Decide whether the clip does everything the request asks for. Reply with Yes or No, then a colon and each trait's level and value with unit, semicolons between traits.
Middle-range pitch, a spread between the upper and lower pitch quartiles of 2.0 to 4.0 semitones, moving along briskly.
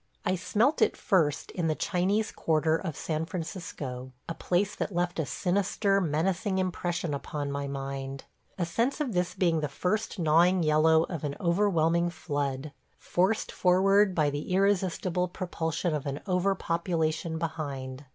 No: medium, 170 Hz; average, 3.5 semitones; average, 160 wpm